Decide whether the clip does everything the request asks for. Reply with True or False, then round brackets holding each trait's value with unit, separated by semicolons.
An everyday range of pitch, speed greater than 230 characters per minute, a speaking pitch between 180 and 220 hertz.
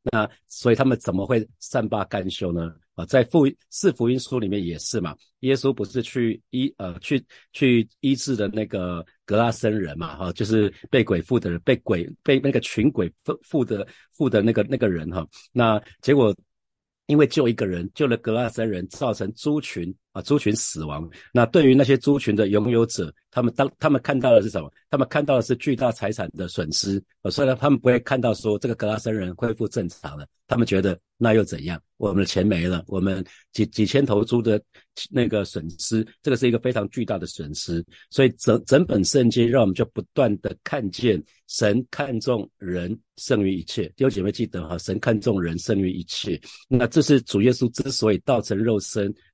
False (4.6 semitones; 295 characters per minute; 110 Hz)